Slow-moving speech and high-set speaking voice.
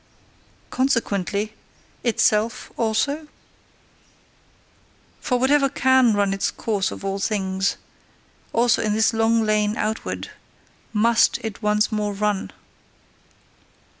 Yes: slow, 100 wpm; high, 215 Hz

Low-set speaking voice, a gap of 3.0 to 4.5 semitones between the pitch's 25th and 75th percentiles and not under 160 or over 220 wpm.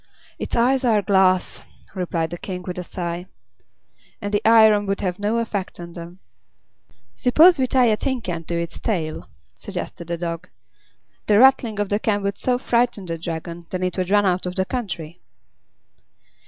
No: high, 190 Hz; average, 4.0 semitones; average, 180 wpm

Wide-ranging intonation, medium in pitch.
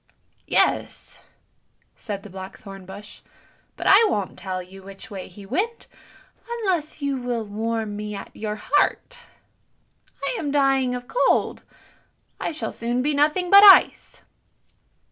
No: wide, 7.0 semitones; high, 240 Hz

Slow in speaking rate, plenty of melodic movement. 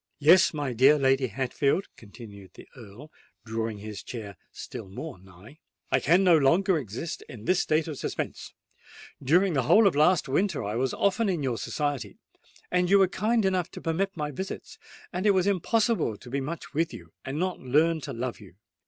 No: average, 180 wpm; wide, 6.9 semitones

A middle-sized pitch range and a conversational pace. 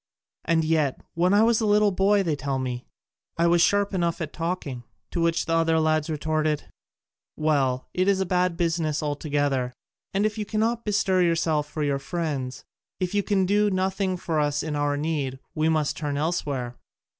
Yes: average, 4.2 semitones; average, 185 wpm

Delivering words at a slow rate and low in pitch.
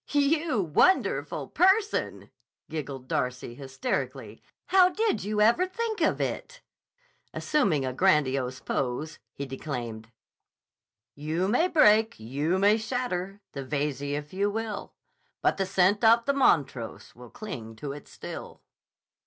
No: slow, 130 wpm; medium, 185 Hz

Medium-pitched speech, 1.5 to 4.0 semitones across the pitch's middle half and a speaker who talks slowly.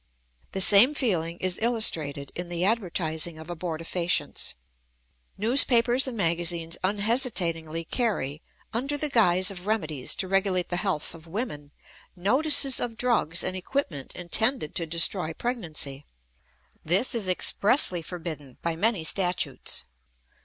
No: medium, 180 Hz; wide, 5.5 semitones; slow, 125 wpm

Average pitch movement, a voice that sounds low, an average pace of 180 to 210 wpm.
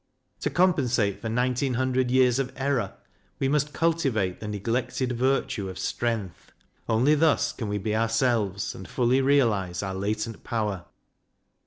No: average, 4.2 semitones; low, 120 Hz; average, 145 wpm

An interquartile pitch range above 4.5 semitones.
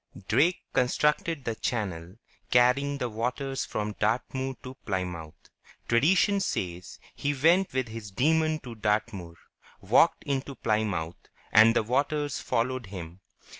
Yes: average, 5.1 semitones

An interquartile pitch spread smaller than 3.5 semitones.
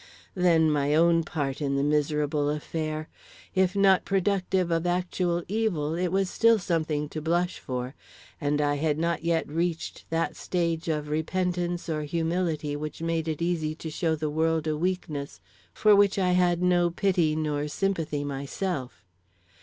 Yes: average, 3.0 semitones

